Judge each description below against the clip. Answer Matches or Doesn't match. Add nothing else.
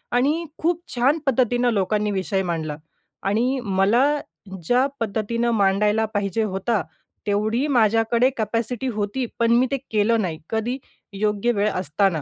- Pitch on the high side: Matches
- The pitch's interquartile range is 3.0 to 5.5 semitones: Matches